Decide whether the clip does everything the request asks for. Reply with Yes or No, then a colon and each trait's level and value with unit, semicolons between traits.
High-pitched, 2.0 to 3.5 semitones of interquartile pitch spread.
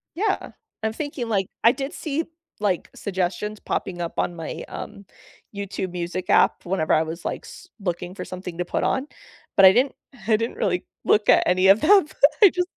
No: high, 200 Hz; wide, 5.5 semitones